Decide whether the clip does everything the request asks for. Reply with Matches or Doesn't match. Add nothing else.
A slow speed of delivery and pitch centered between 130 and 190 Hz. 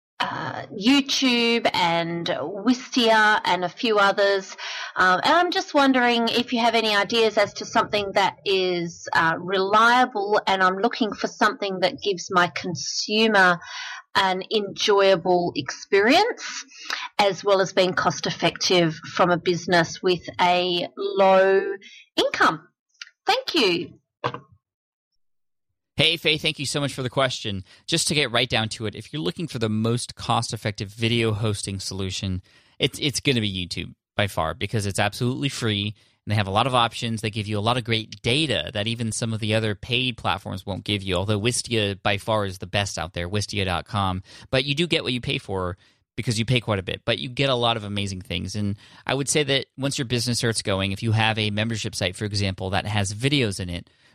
Doesn't match